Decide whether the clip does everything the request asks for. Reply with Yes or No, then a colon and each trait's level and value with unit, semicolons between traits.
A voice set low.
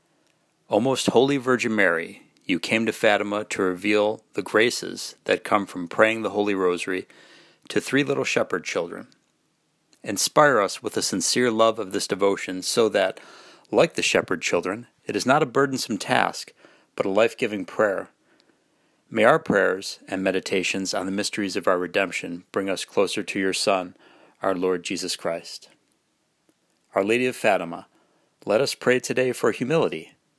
Yes: low, 105 Hz